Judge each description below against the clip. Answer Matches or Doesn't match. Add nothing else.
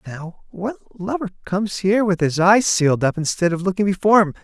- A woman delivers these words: Doesn't match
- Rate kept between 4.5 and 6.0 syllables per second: Matches